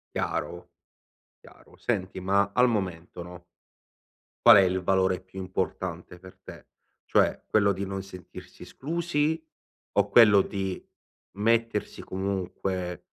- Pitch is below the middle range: Yes, very low, 95 Hz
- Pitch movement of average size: No, narrow, 2.2 semitones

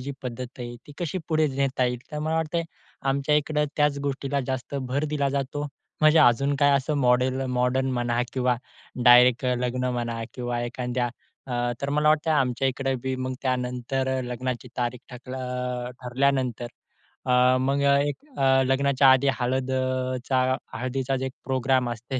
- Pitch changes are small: Yes, narrow, 1.9 semitones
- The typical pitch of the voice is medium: No, low, 130 Hz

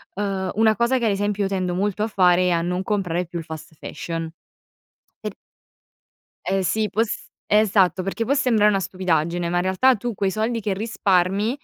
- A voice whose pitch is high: Yes, high, 195 Hz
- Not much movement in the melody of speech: No, average, 3.1 semitones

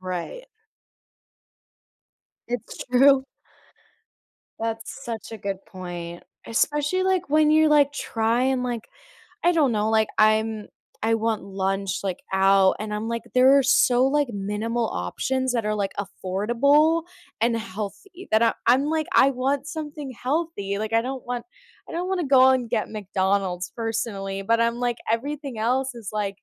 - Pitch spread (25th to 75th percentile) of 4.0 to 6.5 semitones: Yes, average, 4.8 semitones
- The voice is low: No, high, 230 Hz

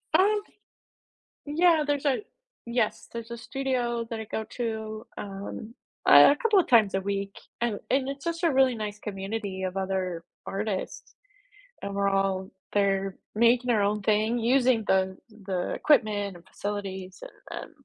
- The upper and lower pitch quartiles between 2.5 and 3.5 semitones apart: No, average, 4.2 semitones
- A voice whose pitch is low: No, high, 215 Hz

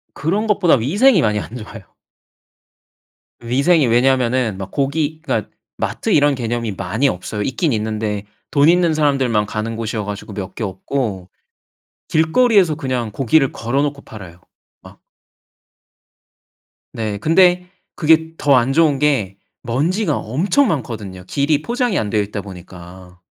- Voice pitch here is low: Yes, low, 130 Hz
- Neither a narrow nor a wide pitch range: No, wide, 6.8 semitones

